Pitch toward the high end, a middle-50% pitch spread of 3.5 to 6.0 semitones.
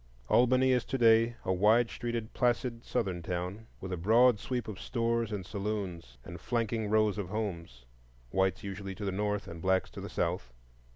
No: low, 105 Hz; average, 3.9 semitones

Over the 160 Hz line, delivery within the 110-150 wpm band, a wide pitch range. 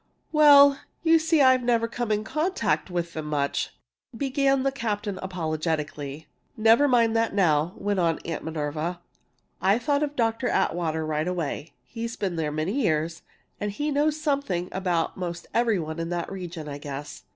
No: high, 190 Hz; average, 165 wpm; wide, 7.5 semitones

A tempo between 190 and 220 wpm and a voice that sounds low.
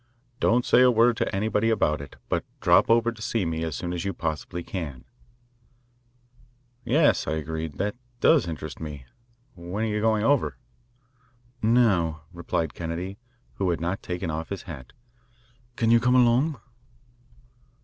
No: average, 155 wpm; very low, 95 Hz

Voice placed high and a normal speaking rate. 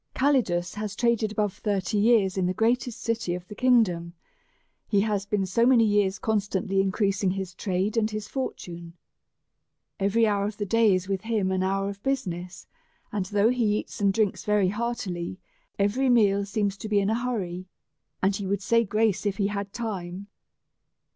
Yes: high, 205 Hz; average, 185 wpm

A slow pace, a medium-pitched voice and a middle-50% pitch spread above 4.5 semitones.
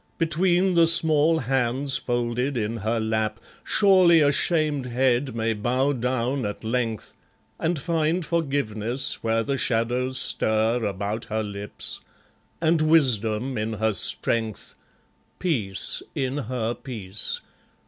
No: slow, 120 wpm; low, 125 Hz; average, 5.1 semitones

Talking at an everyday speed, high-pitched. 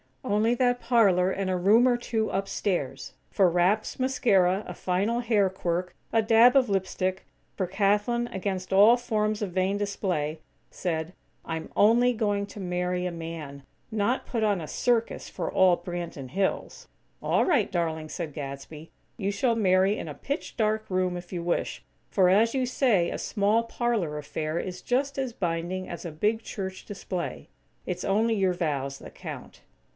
Yes: average, 170 wpm; high, 195 Hz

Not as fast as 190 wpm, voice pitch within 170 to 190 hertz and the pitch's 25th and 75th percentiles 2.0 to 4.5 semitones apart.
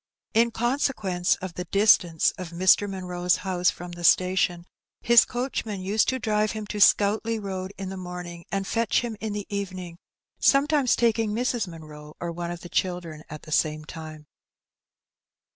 Yes: average, 165 wpm; medium, 185 Hz; average, 3.9 semitones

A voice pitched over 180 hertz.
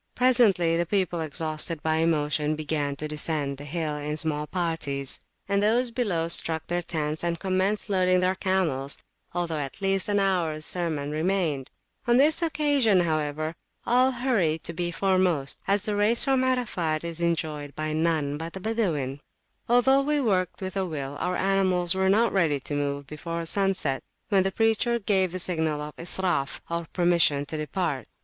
No: medium, 170 Hz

